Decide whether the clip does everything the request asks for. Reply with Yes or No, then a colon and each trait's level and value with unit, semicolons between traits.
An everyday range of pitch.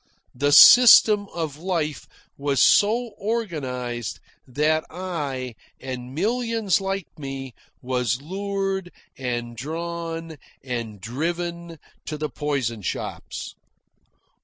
No: wide, 6.4 semitones